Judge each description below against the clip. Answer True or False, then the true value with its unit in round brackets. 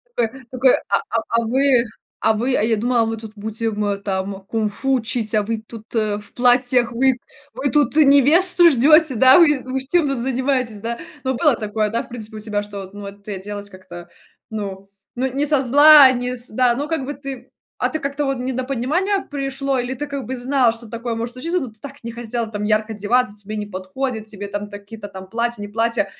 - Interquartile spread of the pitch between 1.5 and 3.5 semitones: False (3.9 semitones)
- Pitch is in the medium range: False (235 Hz)